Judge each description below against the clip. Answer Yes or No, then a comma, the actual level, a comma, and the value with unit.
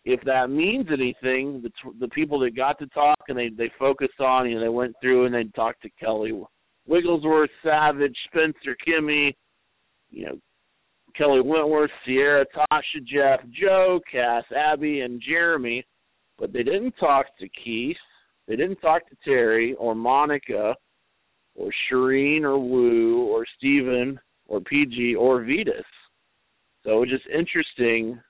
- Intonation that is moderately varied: Yes, average, 3.5 semitones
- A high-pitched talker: No, low, 135 Hz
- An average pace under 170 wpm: Yes, average, 155 wpm